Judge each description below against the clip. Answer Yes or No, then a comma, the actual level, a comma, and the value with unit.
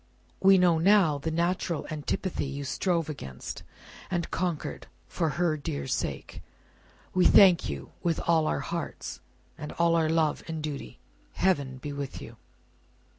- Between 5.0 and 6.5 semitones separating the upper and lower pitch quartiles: No, average, 3.3 semitones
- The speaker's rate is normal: Yes, average, 145 wpm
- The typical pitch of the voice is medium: Yes, medium, 160 Hz